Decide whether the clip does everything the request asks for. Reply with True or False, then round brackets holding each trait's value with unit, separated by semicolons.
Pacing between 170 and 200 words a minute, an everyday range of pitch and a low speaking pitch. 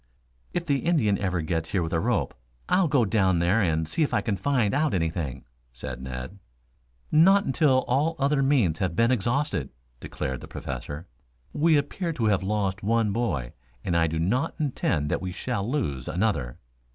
False (180 wpm; 9.0 semitones; 100 Hz)